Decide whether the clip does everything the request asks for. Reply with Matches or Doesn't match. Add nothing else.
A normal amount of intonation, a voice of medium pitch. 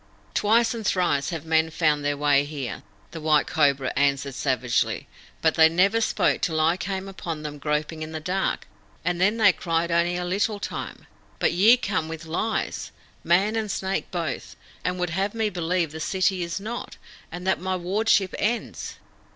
Matches